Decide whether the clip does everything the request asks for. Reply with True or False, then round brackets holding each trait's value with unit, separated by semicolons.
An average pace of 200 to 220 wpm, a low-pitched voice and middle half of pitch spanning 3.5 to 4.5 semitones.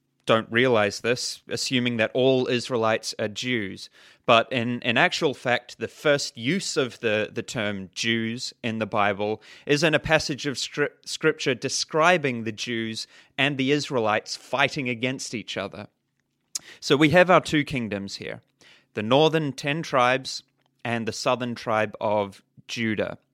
False (150 wpm; 125 Hz; 4.0 semitones)